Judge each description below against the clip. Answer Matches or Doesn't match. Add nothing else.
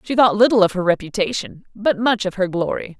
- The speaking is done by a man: Doesn't match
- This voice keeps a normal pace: Doesn't match